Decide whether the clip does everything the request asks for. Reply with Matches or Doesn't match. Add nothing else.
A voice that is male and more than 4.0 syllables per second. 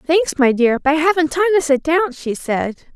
Doesn't match